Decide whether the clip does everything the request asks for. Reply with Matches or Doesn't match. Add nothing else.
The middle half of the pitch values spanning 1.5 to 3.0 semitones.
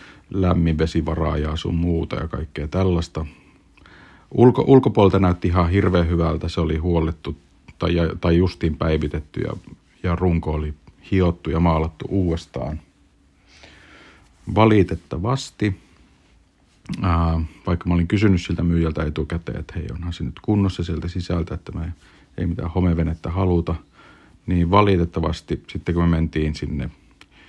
Matches